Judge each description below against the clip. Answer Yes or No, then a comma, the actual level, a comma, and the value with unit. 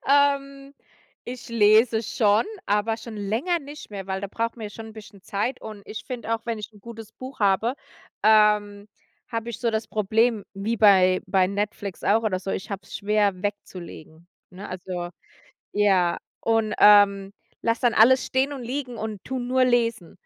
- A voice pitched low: No, high, 215 Hz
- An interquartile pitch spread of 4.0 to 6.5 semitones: No, average, 2.8 semitones